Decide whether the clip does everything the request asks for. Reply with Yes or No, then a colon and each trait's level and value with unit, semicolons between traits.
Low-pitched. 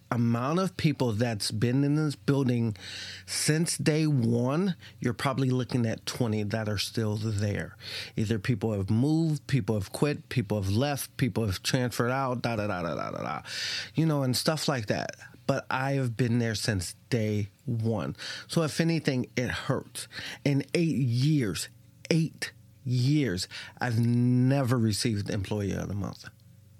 Yes: low, 120 Hz